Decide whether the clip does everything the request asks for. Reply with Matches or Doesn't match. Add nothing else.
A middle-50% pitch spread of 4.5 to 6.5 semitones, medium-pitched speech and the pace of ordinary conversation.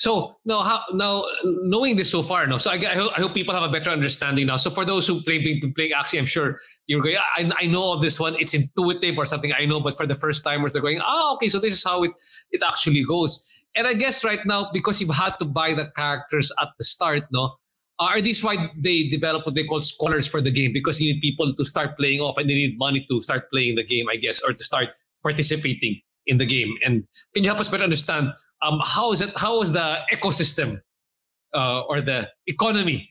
Doesn't match